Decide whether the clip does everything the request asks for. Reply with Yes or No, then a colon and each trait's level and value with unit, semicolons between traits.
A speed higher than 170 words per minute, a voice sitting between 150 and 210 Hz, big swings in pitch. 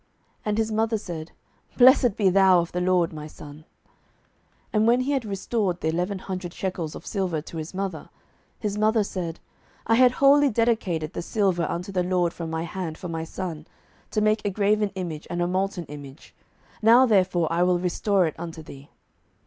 No: average, 190 wpm; medium, 185 Hz; average, 4.1 semitones